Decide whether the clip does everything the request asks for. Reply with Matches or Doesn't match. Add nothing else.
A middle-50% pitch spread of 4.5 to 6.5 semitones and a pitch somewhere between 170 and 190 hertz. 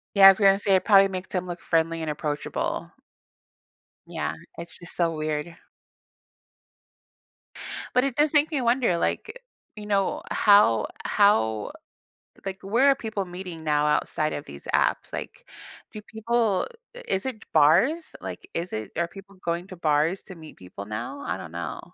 Matches